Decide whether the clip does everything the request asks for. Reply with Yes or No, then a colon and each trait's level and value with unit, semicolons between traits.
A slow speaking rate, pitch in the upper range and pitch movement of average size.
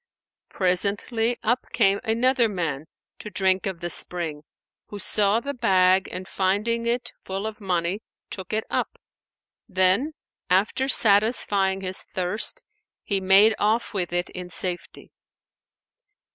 Yes: slow, 130 wpm; high, 195 Hz; average, 3.3 semitones